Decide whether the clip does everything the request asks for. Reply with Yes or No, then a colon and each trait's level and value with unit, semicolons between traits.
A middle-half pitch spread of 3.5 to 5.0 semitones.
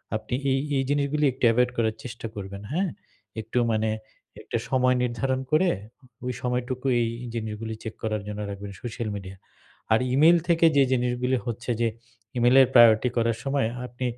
No: average, 2.9 semitones